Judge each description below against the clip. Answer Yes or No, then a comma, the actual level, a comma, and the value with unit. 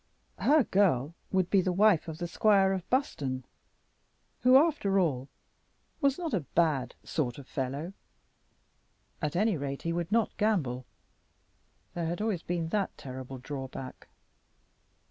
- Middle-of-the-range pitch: Yes, medium, 170 Hz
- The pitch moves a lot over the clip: Yes, wide, 6.9 semitones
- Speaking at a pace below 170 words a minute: Yes, average, 140 wpm